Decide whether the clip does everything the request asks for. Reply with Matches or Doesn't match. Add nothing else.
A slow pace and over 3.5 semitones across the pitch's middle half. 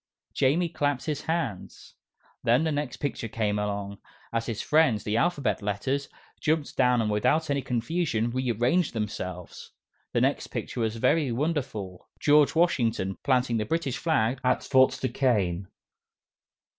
Doesn't match